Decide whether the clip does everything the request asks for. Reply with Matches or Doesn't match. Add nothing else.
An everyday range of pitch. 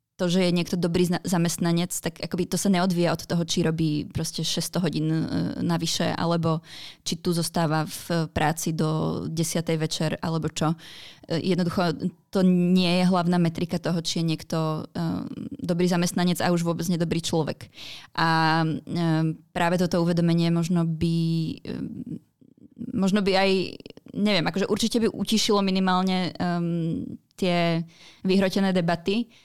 Doesn't match